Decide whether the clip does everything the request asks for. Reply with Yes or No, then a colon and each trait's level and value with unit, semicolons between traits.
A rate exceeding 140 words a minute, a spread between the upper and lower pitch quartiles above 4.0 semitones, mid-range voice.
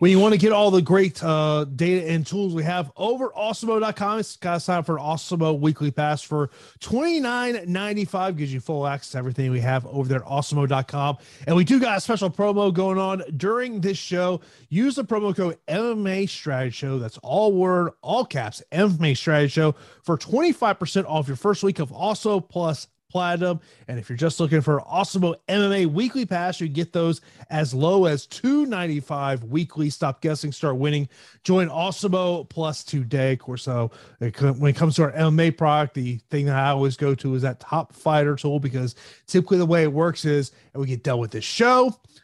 Yes: fast, 205 wpm; average, 5.1 semitones; medium, 160 Hz